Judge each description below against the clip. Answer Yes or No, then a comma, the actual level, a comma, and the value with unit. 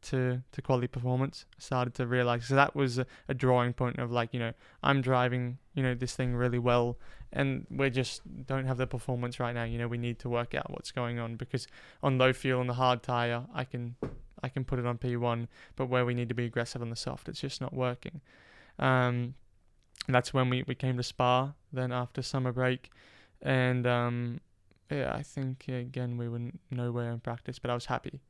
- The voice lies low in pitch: Yes, low, 125 Hz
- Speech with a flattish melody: Yes, narrow, 1.3 semitones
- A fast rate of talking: Yes, fast, 220 wpm